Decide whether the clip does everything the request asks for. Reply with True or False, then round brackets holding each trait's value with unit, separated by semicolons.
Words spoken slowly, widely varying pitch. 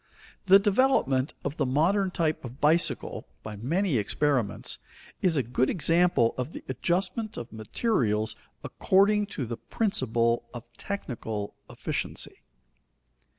True (120 wpm; 8.5 semitones)